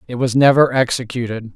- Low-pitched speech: Yes, low, 125 Hz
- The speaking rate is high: No, average, 155 wpm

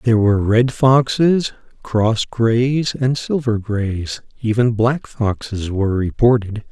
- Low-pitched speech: Yes, low, 115 Hz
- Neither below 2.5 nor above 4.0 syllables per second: Yes, 3.9 syllables/s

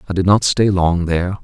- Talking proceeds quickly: Yes, fast, 250 wpm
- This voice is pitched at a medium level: No, very low, 95 Hz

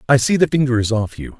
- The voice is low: Yes, low, 120 Hz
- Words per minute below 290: No, fast, 300 wpm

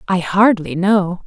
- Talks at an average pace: Yes, average, 145 wpm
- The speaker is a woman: Yes, female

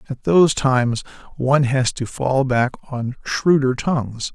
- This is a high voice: No, low, 130 Hz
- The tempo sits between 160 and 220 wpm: No, average, 150 wpm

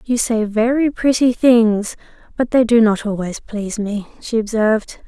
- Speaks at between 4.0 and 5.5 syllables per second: Yes, 4.5 syllables/s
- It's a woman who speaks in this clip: Yes, female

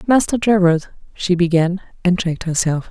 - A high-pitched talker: No, medium, 180 Hz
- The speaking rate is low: Yes, slow, 125 wpm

